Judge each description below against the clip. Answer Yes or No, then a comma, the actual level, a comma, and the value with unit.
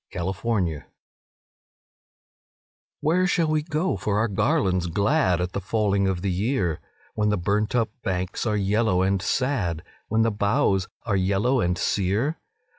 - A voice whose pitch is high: No, low, 100 Hz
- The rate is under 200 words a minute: Yes, average, 160 wpm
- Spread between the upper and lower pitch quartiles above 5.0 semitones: No, average, 4.0 semitones